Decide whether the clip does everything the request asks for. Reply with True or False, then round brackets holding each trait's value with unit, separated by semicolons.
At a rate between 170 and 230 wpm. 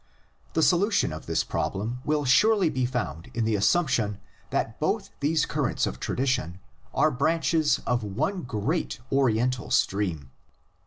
False (145 wpm)